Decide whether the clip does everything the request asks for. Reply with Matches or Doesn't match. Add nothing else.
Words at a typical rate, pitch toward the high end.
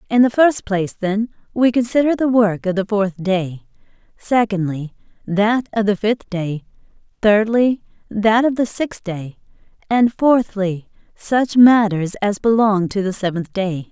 Matches